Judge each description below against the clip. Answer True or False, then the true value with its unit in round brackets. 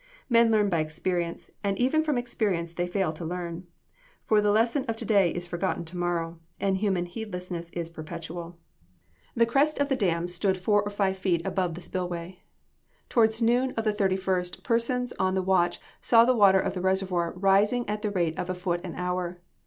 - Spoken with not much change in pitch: False (3.7 semitones)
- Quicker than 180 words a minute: True (200 wpm)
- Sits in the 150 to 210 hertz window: True (190 Hz)